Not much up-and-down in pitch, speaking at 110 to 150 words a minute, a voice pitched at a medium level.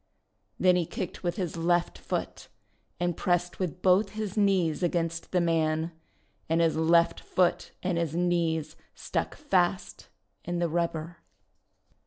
Yes: narrow, 1.5 semitones; average, 140 wpm; medium, 175 Hz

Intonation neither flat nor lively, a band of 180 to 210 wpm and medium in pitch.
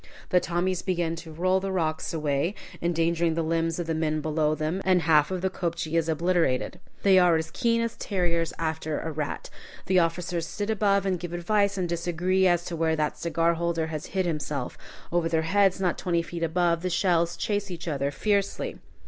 No: narrow, 2.3 semitones; average, 190 wpm; medium, 170 Hz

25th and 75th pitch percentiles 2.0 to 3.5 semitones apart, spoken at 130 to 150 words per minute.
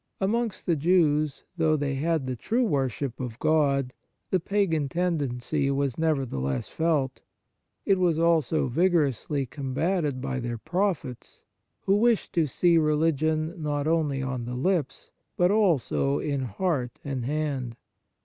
No: average, 4.1 semitones; slow, 135 wpm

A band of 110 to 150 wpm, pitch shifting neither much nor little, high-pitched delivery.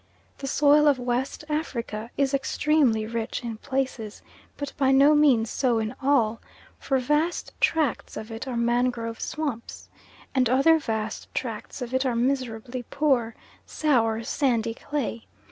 Yes: average, 145 wpm; average, 3.6 semitones; very high, 255 Hz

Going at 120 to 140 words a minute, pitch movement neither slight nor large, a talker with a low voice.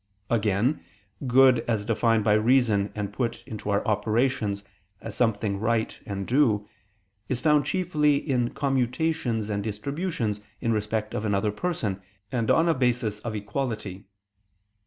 Yes: slow, 135 wpm; average, 4.1 semitones; low, 115 Hz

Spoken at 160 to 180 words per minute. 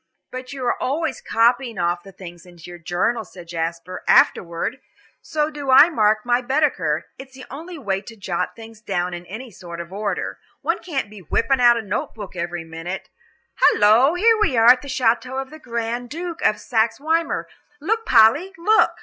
No: average, 190 wpm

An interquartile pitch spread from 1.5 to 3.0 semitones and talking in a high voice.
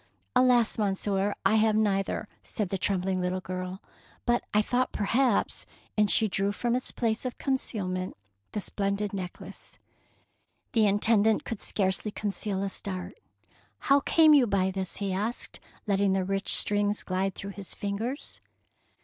Yes: narrow, 2.4 semitones; high, 205 Hz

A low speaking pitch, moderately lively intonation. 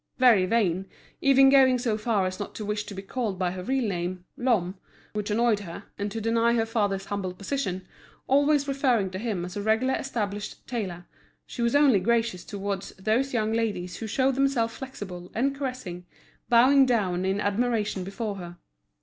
No: high, 215 Hz; average, 4.4 semitones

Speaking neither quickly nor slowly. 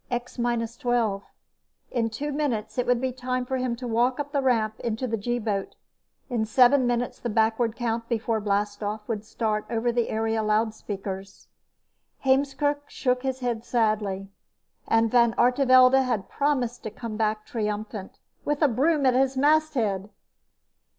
Yes: average, 155 wpm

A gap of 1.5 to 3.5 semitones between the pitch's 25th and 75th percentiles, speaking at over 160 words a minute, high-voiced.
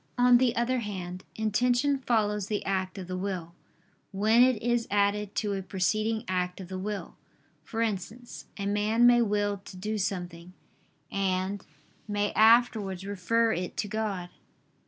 No: average, 3.2 semitones; average, 155 wpm; high, 205 Hz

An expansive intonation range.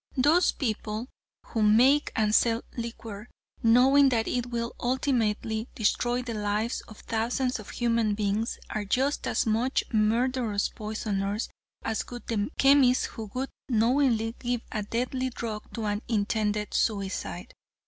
No: average, 2.7 semitones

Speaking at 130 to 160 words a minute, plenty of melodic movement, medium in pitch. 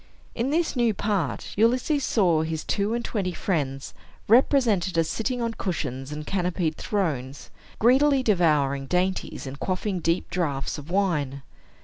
Yes: average, 140 wpm; wide, 6.7 semitones; medium, 180 Hz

